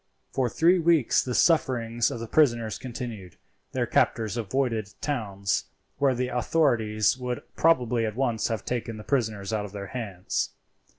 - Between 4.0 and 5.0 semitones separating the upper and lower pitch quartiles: No, average, 3.1 semitones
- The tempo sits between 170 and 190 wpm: No, average, 155 wpm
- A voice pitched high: No, low, 120 Hz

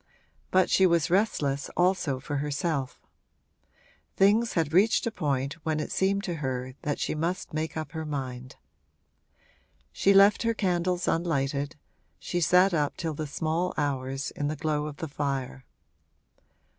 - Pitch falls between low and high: Yes, medium, 155 Hz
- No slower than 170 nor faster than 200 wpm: No, average, 150 wpm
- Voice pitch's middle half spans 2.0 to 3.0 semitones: No, average, 4.2 semitones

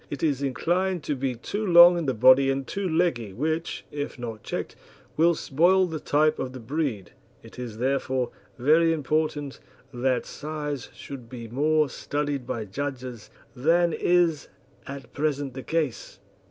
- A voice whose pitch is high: No, medium, 145 Hz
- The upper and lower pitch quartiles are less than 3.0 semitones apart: No, average, 3.8 semitones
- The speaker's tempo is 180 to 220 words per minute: No, average, 155 wpm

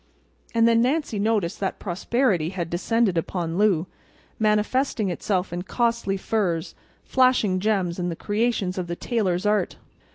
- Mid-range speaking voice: No, high, 200 Hz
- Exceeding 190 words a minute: No, slow, 135 wpm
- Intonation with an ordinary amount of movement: Yes, average, 4.3 semitones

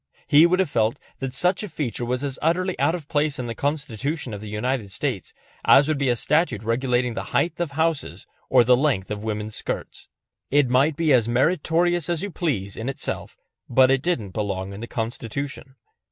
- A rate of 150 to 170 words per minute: No, average, 200 wpm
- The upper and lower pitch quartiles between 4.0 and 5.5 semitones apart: Yes, average, 5.2 semitones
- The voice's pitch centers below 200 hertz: Yes, low, 135 Hz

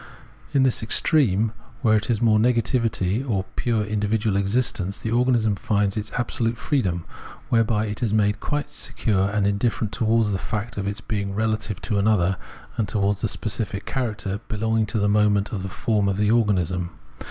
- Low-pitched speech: Yes, low, 105 Hz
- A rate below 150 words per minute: No, average, 185 wpm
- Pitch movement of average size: No, narrow, 2.2 semitones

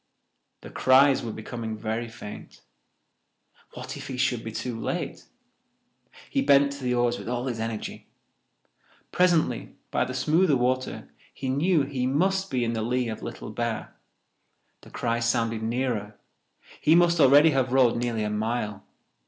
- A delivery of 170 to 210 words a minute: No, average, 155 wpm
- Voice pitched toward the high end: No, low, 125 Hz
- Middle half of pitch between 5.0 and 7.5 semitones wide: No, average, 3.2 semitones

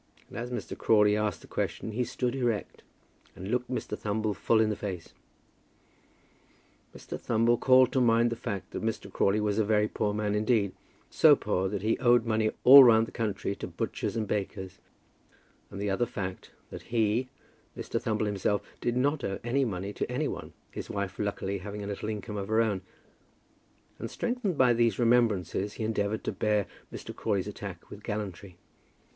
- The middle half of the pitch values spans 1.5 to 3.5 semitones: Yes, average, 2.7 semitones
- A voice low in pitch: Yes, low, 110 Hz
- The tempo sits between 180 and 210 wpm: Yes, average, 185 wpm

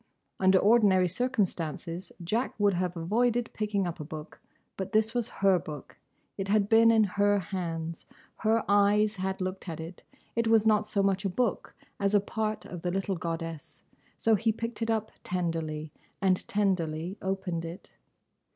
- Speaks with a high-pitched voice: Yes, high, 195 Hz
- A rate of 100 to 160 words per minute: No, average, 170 wpm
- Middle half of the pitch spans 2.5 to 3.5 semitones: No, average, 3.9 semitones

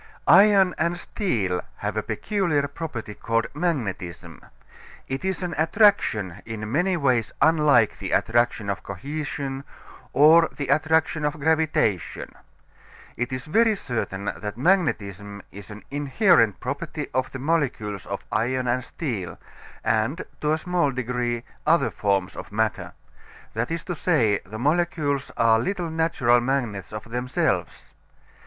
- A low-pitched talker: Yes, low, 130 Hz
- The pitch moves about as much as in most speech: No, wide, 6.5 semitones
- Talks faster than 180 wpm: No, slow, 135 wpm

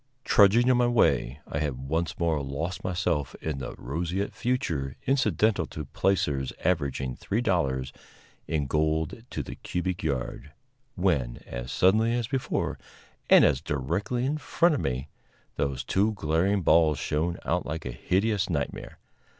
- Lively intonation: Yes, wide, 6.0 semitones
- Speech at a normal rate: Yes, average, 150 wpm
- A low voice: Yes, very low, 80 Hz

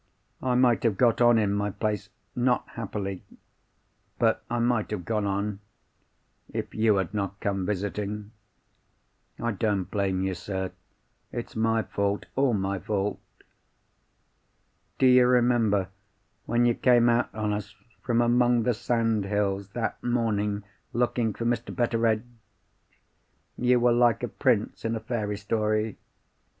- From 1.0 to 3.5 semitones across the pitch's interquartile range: Yes, average, 2.8 semitones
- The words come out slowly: Yes, slow, 130 wpm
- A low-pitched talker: Yes, low, 110 Hz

